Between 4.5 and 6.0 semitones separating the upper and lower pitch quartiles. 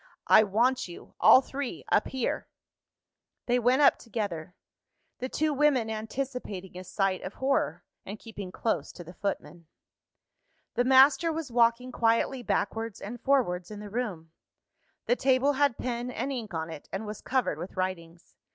Yes: wide, 5.5 semitones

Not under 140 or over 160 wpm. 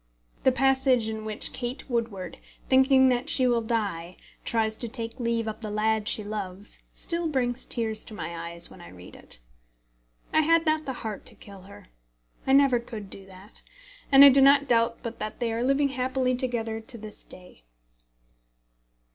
No: average, 180 wpm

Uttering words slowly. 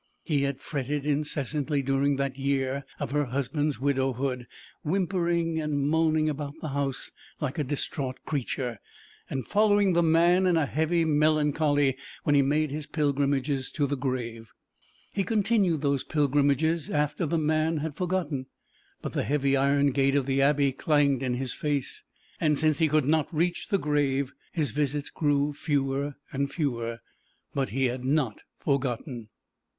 No: average, 155 wpm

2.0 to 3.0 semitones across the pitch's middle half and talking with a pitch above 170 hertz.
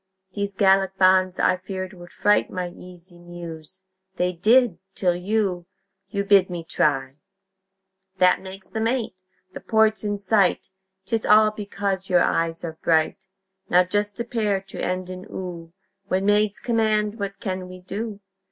Yes: narrow, 2.6 semitones; high, 190 Hz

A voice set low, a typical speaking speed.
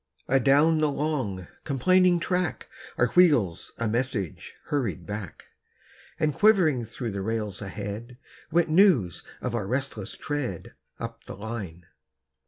No: low, 125 Hz; slow, 125 wpm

